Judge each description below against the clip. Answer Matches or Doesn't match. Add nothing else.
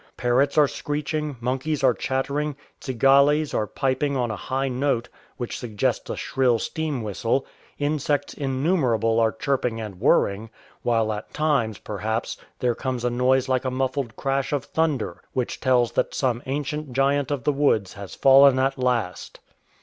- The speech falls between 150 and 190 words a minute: Matches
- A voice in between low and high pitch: Doesn't match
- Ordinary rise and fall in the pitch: Matches